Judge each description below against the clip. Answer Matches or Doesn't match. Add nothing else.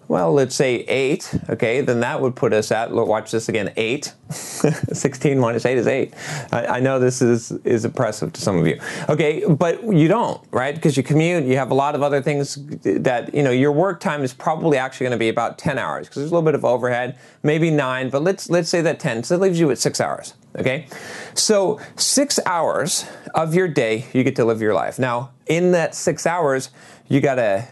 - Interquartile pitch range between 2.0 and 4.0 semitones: Doesn't match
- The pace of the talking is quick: Matches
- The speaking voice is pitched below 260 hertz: Matches